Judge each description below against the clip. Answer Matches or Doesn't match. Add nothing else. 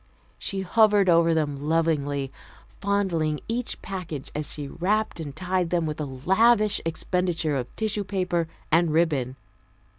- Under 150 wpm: Matches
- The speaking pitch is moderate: Matches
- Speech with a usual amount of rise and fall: Matches